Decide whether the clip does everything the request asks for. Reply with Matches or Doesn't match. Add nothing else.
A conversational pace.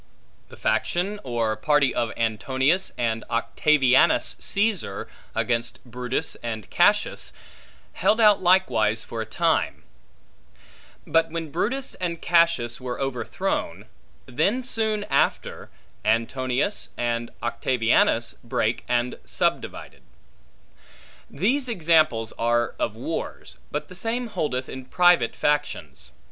Doesn't match